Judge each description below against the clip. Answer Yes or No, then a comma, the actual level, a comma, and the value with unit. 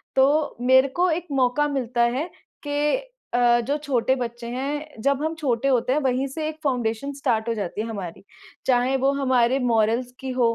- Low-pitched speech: No, very high, 260 Hz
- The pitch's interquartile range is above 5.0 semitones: No, average, 3.0 semitones